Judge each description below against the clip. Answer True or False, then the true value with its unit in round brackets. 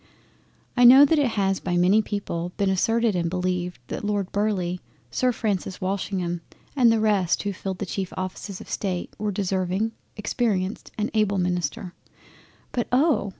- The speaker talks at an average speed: True (170 wpm)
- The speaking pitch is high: True (195 Hz)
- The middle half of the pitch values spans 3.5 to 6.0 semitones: False (3.0 semitones)